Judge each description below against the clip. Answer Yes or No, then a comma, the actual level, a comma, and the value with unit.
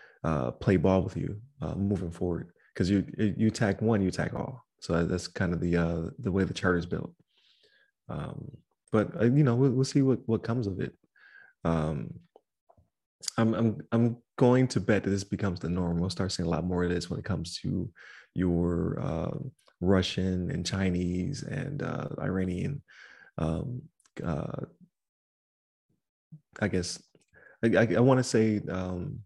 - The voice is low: Yes, very low, 95 Hz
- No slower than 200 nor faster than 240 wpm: No, average, 170 wpm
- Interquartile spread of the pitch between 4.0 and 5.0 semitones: Yes, average, 4.4 semitones